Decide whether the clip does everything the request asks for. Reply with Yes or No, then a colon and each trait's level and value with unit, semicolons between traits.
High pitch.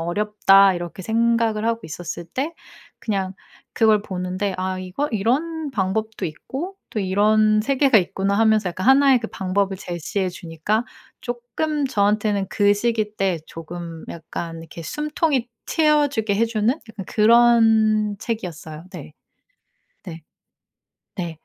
Yes: high, 210 Hz